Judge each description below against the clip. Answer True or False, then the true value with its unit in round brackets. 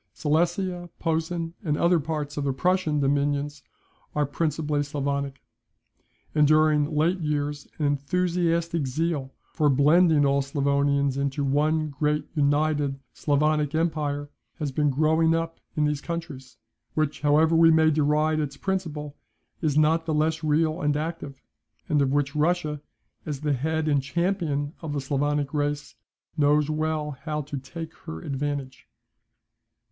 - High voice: False (150 Hz)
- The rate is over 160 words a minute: False (140 wpm)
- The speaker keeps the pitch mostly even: True (1.9 semitones)